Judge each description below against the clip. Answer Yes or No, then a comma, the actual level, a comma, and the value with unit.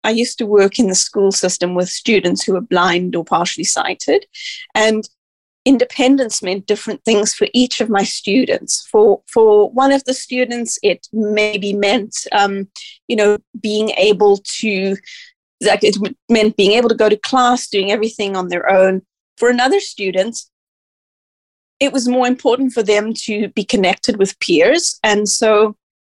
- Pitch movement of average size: Yes, average, 3.9 semitones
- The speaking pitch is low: No, high, 215 Hz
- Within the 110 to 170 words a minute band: Yes, average, 160 wpm